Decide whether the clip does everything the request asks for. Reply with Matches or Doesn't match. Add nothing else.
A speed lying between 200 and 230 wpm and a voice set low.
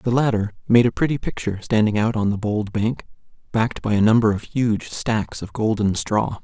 Matches